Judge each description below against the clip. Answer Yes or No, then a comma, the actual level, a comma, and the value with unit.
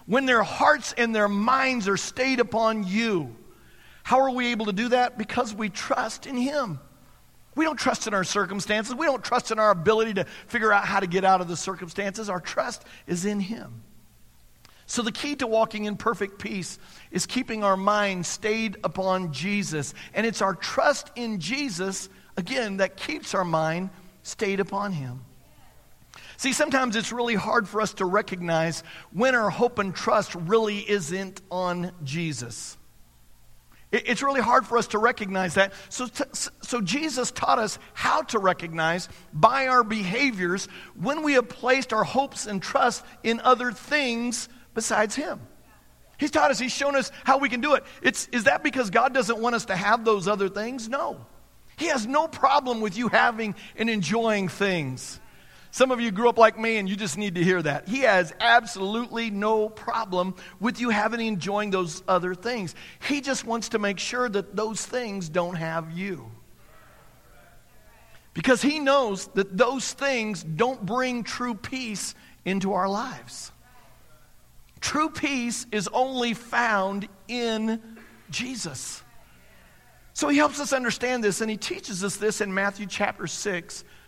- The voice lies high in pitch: Yes, high, 215 Hz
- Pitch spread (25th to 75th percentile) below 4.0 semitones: No, average, 4.5 semitones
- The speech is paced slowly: No, average, 170 wpm